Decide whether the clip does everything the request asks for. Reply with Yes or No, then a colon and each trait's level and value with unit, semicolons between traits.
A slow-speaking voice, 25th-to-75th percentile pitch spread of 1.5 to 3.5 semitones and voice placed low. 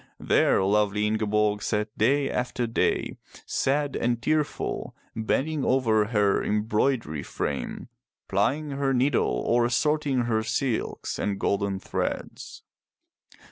No: slow, 110 wpm; average, 4.3 semitones; low, 115 Hz